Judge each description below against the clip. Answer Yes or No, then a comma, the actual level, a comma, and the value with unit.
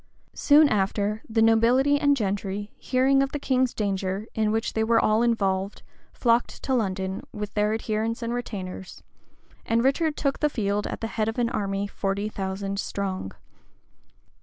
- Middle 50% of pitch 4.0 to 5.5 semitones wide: No, average, 3.5 semitones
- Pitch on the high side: Yes, high, 220 Hz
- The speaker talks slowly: No, average, 165 wpm